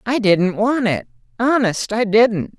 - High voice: Yes, high, 220 Hz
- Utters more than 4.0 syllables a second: No, 3.8 syllables/s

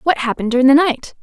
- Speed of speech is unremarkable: No, fast, 245 wpm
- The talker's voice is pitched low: No, very high, 270 Hz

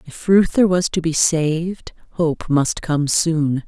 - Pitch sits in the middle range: Yes, medium, 165 Hz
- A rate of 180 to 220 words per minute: No, average, 165 wpm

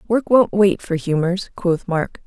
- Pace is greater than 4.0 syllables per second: No, 3.9 syllables/s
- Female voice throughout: Yes, female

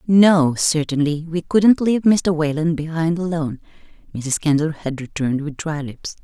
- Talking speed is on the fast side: No, average, 155 wpm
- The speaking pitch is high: No, medium, 160 Hz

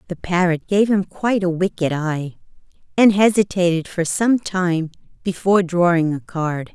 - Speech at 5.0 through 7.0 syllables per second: No, 4.7 syllables/s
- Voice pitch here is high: No, medium, 180 Hz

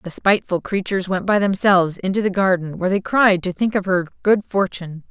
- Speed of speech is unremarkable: No, fast, 210 wpm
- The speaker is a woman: Yes, female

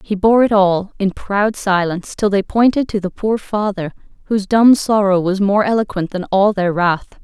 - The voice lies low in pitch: No, high, 200 Hz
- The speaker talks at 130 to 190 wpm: No, average, 200 wpm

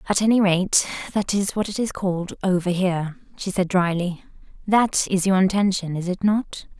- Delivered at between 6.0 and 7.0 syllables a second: No, 5.1 syllables/s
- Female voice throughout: Yes, female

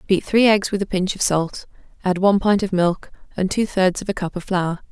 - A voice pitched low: No, high, 190 Hz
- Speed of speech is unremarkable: No, fast, 255 wpm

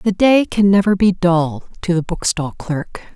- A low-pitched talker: No, medium, 185 Hz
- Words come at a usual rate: Yes, average, 190 wpm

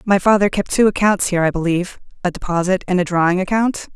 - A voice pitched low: No, medium, 185 Hz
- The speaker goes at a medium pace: Yes, average, 195 wpm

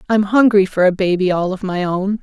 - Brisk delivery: Yes, fast, 240 wpm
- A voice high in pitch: Yes, high, 195 Hz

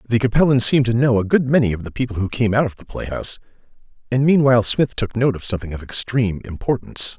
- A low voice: Yes, low, 115 Hz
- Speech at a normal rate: No, fast, 225 wpm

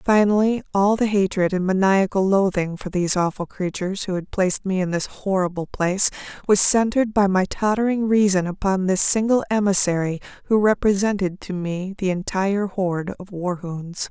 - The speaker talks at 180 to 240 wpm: No, average, 160 wpm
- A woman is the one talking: Yes, female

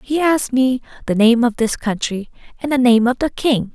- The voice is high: Yes, high, 245 Hz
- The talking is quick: Yes, fast, 225 wpm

